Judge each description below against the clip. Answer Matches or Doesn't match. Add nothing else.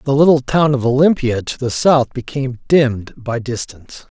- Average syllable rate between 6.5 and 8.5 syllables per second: Doesn't match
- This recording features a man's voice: Matches